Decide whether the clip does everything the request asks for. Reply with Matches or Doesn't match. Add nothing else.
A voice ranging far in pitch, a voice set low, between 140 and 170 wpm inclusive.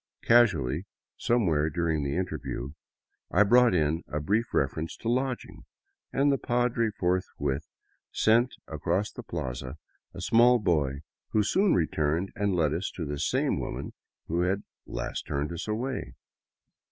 Matches